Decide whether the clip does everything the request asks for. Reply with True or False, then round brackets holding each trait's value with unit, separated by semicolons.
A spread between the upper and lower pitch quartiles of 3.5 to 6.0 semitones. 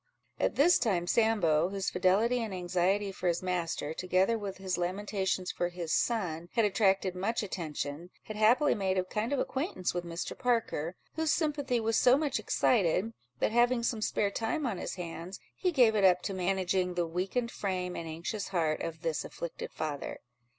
True (4.3 semitones)